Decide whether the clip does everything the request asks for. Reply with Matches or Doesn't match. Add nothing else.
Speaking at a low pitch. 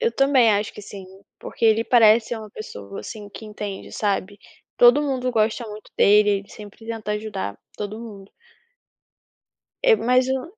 Doesn't match